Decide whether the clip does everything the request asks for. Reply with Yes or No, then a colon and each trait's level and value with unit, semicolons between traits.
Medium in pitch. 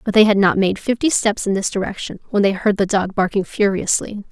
No: high, 200 Hz